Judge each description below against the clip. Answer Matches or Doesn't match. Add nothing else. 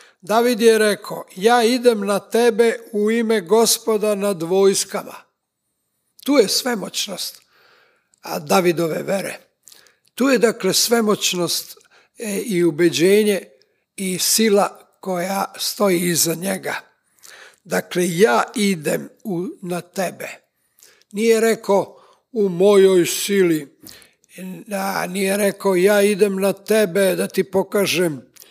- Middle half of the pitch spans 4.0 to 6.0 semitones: Doesn't match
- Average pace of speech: Doesn't match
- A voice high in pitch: Matches